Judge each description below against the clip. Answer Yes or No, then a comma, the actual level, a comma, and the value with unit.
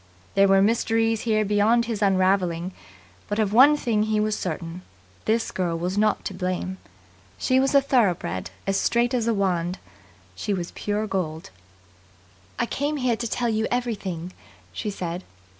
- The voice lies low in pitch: No, high, 205 Hz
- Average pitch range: Yes, average, 3.8 semitones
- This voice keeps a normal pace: Yes, average, 160 wpm